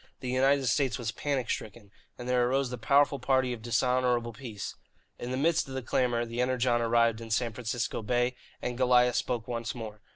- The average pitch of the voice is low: Yes, low, 125 Hz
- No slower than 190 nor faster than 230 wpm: Yes, average, 195 wpm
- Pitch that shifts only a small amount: Yes, narrow, 1.7 semitones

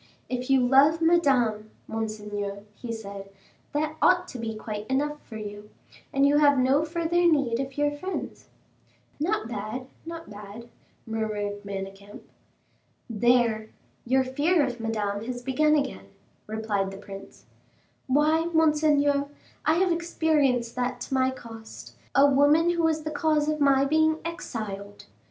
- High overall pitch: Yes, very high, 260 Hz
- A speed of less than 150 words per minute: Yes, average, 140 wpm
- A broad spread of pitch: Yes, wide, 5.8 semitones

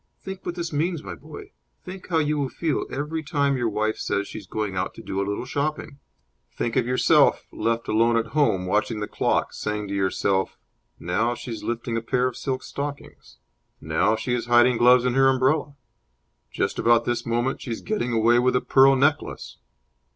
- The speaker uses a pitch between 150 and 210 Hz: No, low, 120 Hz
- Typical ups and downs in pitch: Yes, average, 4.4 semitones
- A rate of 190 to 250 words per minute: Yes, average, 200 wpm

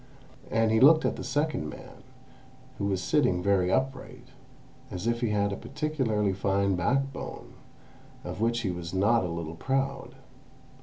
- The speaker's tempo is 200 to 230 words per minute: No, average, 155 wpm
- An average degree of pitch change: No, wide, 5.9 semitones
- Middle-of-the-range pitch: No, low, 105 Hz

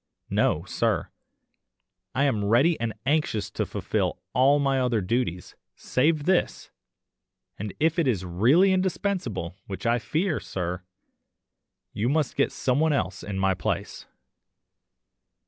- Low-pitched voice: Yes, low, 125 Hz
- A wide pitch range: Yes, wide, 7.4 semitones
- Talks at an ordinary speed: No, slow, 130 wpm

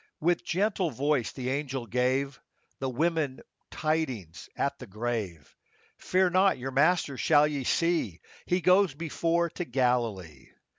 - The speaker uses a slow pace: No, average, 145 wpm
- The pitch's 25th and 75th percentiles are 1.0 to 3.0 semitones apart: No, average, 5.2 semitones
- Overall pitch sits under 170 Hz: Yes, medium, 140 Hz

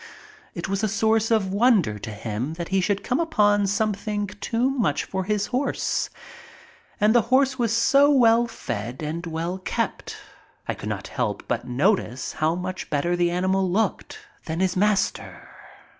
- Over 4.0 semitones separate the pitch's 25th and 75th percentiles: Yes, average, 4.6 semitones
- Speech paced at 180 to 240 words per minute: No, average, 165 wpm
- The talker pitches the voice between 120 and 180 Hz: No, high, 195 Hz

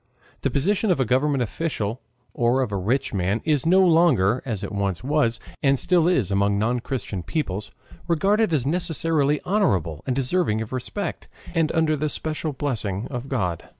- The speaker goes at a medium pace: Yes, average, 175 wpm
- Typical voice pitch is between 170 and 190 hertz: No, low, 135 Hz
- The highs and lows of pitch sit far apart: Yes, wide, 7.1 semitones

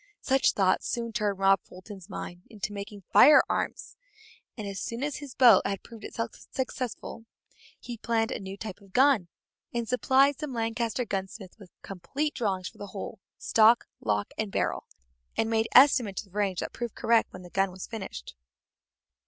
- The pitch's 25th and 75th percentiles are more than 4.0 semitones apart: No, average, 3.6 semitones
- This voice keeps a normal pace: Yes, average, 170 wpm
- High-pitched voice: Yes, high, 220 Hz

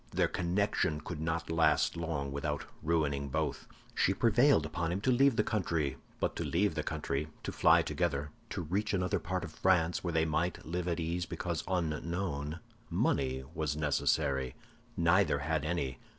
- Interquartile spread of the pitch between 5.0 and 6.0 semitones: No, average, 3.2 semitones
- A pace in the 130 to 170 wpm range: Yes, average, 165 wpm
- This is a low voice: Yes, very low, 80 Hz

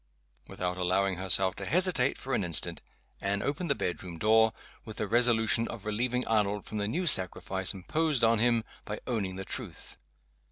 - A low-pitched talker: Yes, low, 110 Hz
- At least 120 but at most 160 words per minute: No, average, 170 wpm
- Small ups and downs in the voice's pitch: No, average, 4.2 semitones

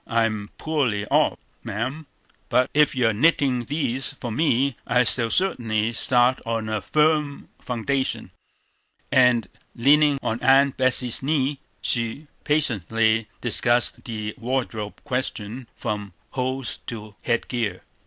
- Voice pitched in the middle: No, low, 125 Hz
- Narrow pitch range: No, average, 3.3 semitones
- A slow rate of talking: Yes, slow, 125 wpm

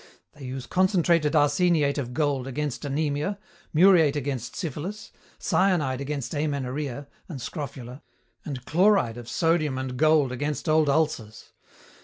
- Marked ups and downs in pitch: No, average, 3.3 semitones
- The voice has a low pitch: No, medium, 145 Hz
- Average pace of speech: No, slow, 125 wpm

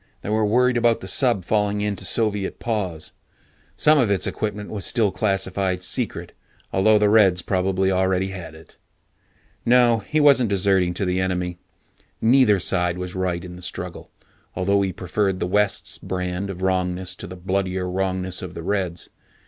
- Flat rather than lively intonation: Yes, narrow, 2.3 semitones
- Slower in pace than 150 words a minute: No, average, 165 wpm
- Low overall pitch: Yes, very low, 95 Hz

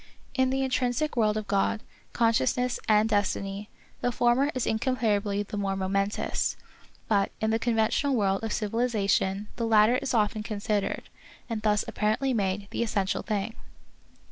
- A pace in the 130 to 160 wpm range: Yes, average, 155 wpm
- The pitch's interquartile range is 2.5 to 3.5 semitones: Yes, average, 2.8 semitones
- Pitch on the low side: No, high, 215 Hz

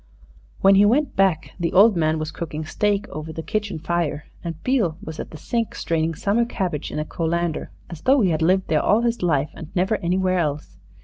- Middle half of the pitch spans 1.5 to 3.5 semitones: No, average, 4.3 semitones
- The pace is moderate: No, fast, 210 wpm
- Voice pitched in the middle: Yes, medium, 175 Hz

